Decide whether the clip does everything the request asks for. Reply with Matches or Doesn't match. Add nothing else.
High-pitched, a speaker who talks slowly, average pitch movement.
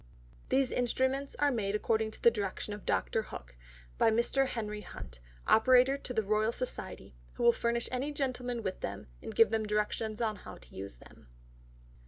Doesn't match